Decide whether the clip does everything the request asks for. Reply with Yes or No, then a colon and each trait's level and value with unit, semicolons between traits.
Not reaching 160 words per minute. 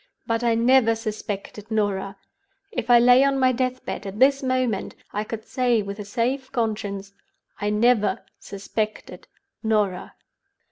Yes: average, 145 wpm